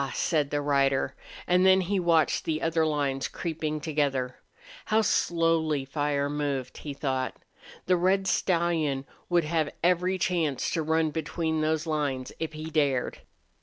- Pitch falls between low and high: Yes, medium, 155 Hz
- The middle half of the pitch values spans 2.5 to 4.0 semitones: Yes, average, 2.9 semitones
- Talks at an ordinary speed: Yes, average, 145 wpm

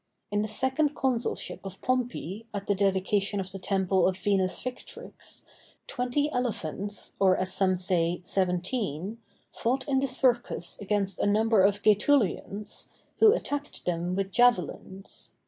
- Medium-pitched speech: No, high, 205 Hz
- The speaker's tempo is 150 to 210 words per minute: No, average, 140 wpm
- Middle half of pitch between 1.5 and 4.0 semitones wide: No, average, 4.6 semitones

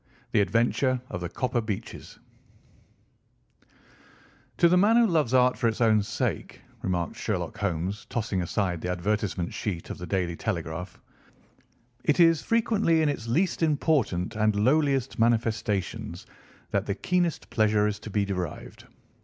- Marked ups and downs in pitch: Yes, wide, 6.8 semitones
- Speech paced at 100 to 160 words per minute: Yes, average, 145 wpm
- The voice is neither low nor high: No, low, 110 Hz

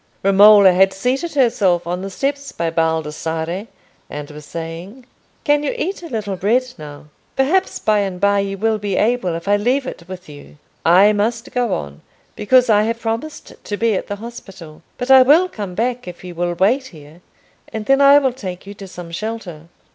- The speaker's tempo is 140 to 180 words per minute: No, average, 195 wpm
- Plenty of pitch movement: Yes, wide, 5.8 semitones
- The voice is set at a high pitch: Yes, high, 205 Hz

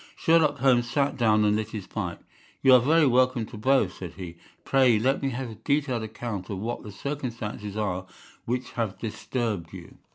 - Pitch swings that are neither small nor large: Yes, average, 4.0 semitones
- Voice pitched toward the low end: Yes, low, 115 Hz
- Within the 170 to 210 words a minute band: Yes, average, 190 wpm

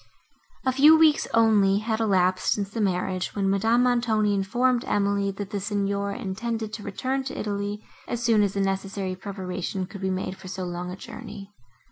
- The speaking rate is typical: Yes, average, 180 wpm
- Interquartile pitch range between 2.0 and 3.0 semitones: Yes, average, 2.7 semitones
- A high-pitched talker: Yes, high, 200 Hz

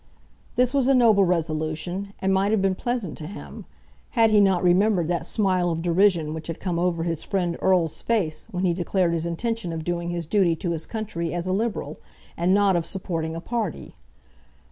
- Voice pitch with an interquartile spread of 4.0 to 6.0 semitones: No, average, 3.2 semitones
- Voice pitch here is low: No, medium, 180 Hz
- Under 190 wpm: No, average, 200 wpm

